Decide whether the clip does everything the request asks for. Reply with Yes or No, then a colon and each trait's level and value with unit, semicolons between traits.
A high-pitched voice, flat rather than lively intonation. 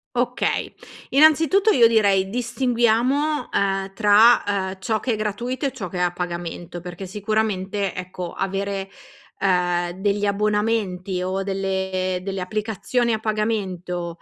No: high, 200 Hz; average, 3.2 semitones